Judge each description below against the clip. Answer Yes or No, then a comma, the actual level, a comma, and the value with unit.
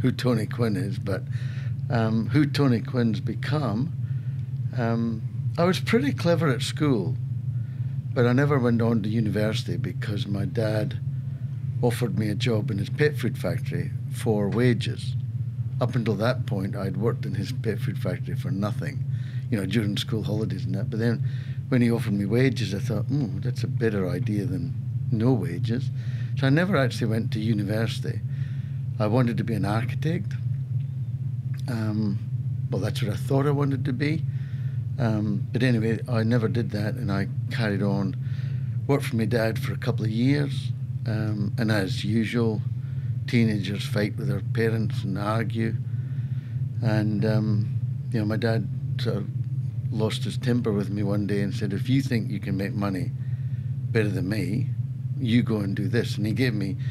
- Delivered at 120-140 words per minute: No, average, 175 wpm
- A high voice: No, low, 125 Hz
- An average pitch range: No, narrow, 2.1 semitones